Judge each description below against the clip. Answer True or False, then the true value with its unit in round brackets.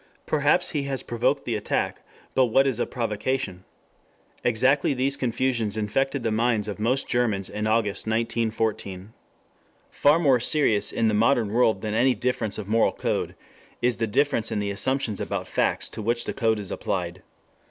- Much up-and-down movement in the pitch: False (3.5 semitones)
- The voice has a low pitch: True (115 Hz)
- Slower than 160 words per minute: False (170 wpm)